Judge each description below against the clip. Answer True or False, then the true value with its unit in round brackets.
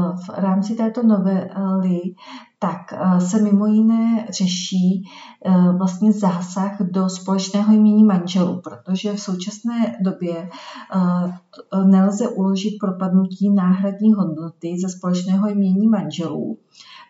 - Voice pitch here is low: False (190 Hz)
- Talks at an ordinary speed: False (100 wpm)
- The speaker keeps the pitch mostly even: True (2.1 semitones)